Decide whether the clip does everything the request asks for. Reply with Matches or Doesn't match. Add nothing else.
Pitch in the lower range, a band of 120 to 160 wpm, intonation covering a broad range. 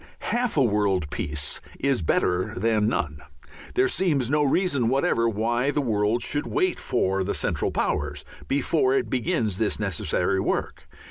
Matches